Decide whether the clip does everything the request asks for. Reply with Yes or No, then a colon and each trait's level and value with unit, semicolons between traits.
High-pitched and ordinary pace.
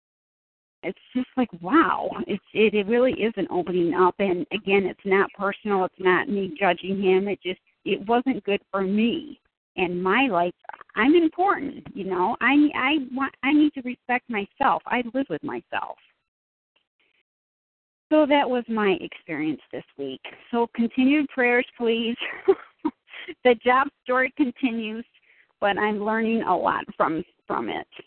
Yes: high, 235 Hz; average, 150 wpm